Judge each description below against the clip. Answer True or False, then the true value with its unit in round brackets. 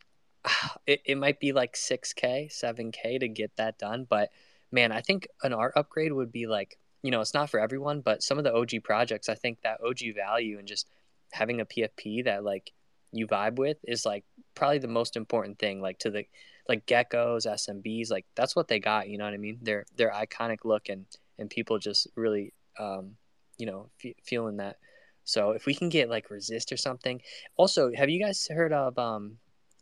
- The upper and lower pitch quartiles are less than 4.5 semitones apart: True (3.5 semitones)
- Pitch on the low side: True (115 Hz)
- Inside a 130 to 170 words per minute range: False (205 wpm)